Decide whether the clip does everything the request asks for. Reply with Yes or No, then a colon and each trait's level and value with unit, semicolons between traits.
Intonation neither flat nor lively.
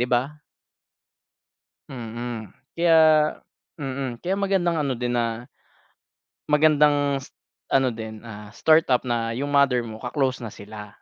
Yes: average, 3.8 semitones